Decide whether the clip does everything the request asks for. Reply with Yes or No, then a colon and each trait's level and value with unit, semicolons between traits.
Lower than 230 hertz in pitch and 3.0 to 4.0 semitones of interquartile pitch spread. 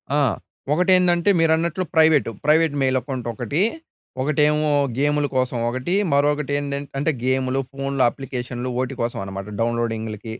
Yes: medium, 140 Hz; average, 3.4 semitones